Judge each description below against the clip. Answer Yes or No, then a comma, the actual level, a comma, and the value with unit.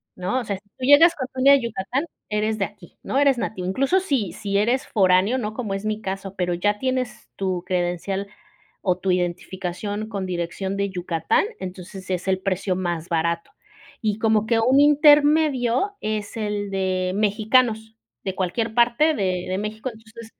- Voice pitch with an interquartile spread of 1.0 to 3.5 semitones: No, average, 4.3 semitones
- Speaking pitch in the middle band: No, high, 205 Hz